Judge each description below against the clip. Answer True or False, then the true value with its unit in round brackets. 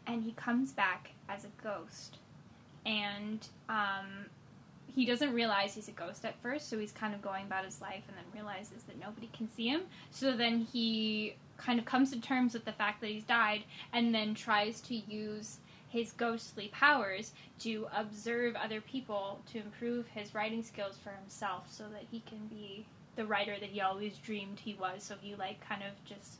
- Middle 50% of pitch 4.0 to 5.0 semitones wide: False (2.4 semitones)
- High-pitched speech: True (215 Hz)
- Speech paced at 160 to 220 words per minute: True (195 wpm)